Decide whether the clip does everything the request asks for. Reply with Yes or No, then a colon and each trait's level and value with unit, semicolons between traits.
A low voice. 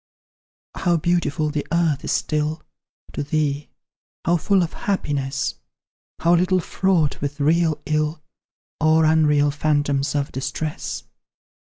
No: medium, 155 Hz